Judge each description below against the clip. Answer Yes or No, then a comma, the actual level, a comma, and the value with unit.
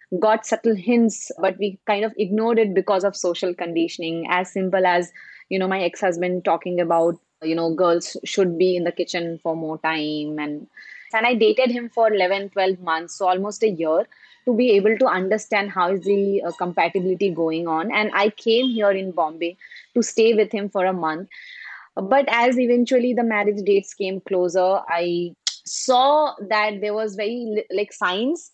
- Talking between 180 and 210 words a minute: Yes, average, 185 wpm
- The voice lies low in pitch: No, high, 195 Hz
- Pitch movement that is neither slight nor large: Yes, average, 3.6 semitones